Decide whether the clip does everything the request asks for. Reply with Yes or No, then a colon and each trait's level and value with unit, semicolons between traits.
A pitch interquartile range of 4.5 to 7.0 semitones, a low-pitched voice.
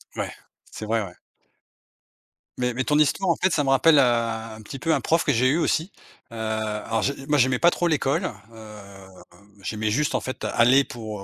Yes: average, 5.2 semitones; low, 125 Hz